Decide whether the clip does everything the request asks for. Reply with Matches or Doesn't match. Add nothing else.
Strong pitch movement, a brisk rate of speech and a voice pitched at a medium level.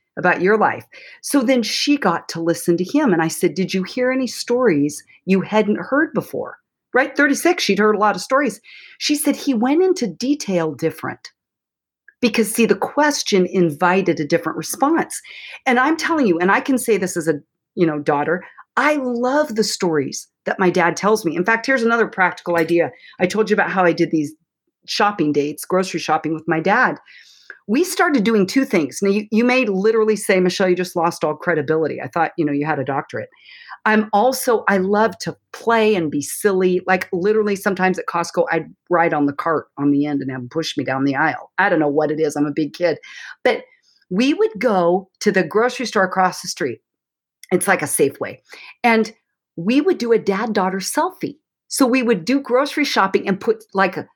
Doesn't match